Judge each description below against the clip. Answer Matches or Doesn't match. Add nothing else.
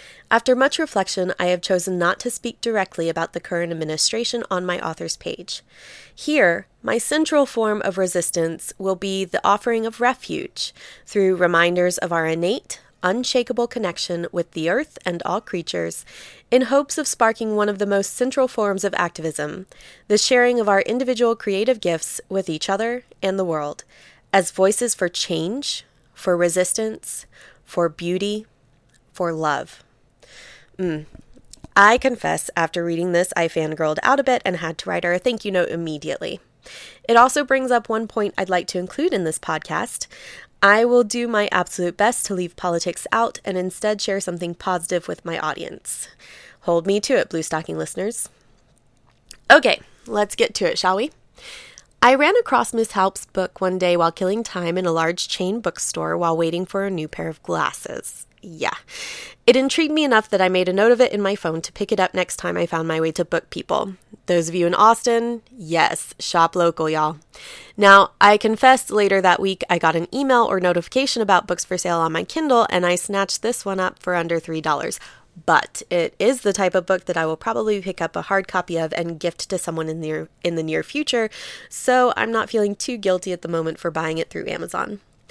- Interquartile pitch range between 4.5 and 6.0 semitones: Matches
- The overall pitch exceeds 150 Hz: Matches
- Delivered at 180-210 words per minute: Matches